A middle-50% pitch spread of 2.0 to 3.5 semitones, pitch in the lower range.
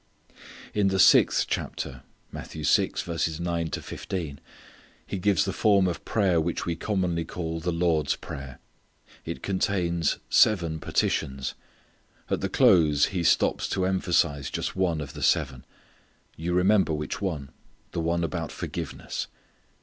Yes: average, 2.9 semitones; very low, 85 Hz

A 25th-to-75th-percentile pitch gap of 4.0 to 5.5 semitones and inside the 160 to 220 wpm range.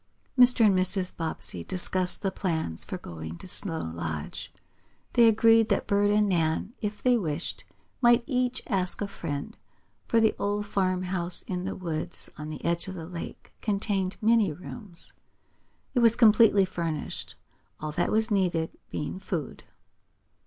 No: average, 4.4 semitones; average, 150 wpm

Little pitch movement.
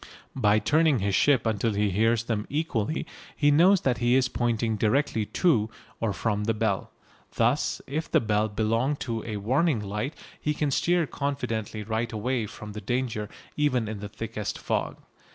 No: average, 4.4 semitones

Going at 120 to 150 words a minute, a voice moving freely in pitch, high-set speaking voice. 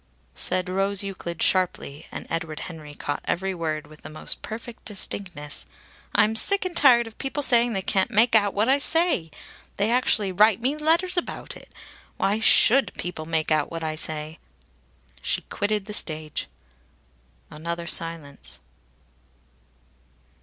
Yes: average, 145 wpm; wide, 6.0 semitones; high, 195 Hz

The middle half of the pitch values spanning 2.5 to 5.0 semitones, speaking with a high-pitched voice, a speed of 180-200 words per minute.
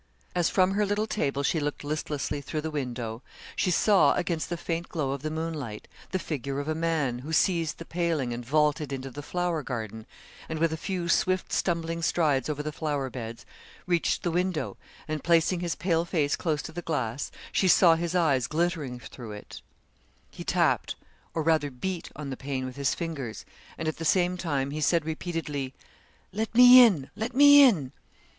No: average, 3.9 semitones; medium, 160 Hz; average, 190 wpm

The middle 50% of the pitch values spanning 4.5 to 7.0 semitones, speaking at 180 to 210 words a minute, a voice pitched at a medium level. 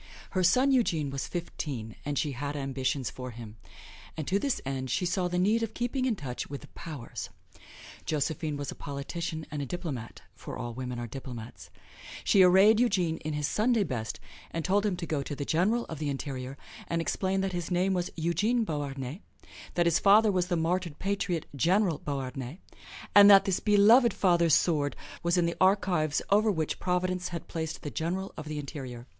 Yes: average, 5.2 semitones; average, 190 wpm; medium, 165 Hz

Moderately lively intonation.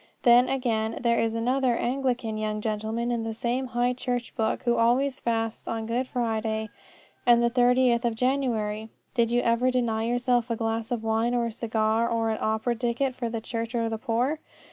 No: narrow, 1.6 semitones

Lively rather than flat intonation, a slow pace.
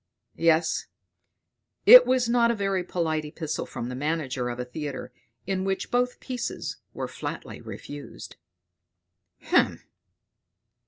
Yes: wide, 8.2 semitones; slow, 120 wpm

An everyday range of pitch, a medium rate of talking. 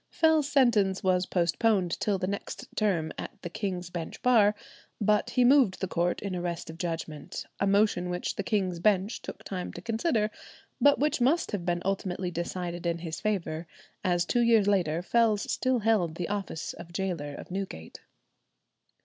Yes: average, 3.7 semitones; average, 175 wpm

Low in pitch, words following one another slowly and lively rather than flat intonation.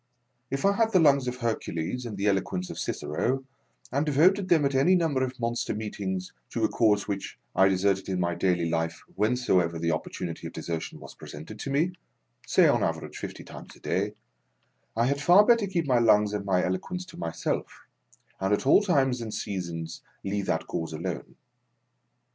No: low, 105 Hz; average, 190 wpm; wide, 7.3 semitones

